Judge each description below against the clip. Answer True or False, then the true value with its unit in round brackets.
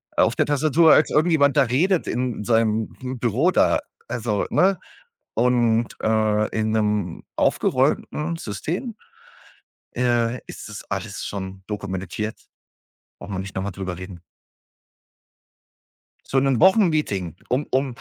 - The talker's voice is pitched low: True (115 Hz)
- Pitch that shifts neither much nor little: False (6.1 semitones)